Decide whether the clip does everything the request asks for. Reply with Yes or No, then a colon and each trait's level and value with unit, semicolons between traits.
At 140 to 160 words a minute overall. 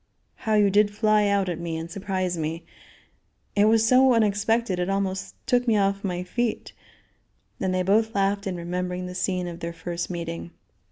No: average, 180 wpm